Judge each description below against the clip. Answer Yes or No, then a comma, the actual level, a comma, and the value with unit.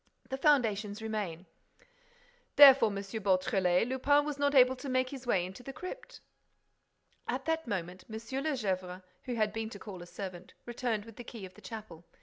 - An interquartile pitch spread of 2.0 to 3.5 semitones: No, wide, 5.4 semitones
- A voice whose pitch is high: Yes, high, 220 Hz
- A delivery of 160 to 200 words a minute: Yes, average, 180 wpm